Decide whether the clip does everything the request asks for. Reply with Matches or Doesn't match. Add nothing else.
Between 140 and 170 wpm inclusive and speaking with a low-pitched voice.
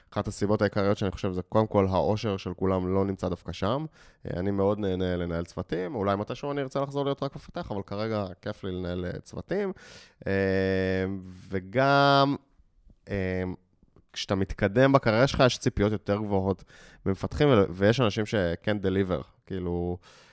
Matches